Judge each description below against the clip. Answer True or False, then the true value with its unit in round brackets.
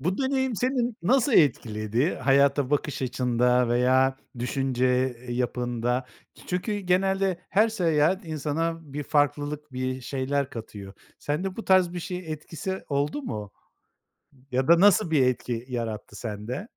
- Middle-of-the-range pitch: True (145 Hz)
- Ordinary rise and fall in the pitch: False (6.4 semitones)